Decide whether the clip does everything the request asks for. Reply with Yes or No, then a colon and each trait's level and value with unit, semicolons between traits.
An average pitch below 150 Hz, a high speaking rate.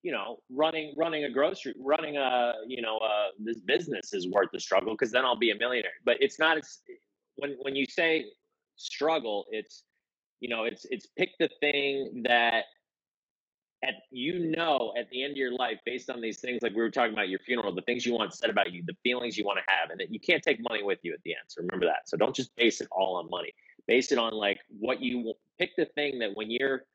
Yes: low, 135 Hz; fast, 245 wpm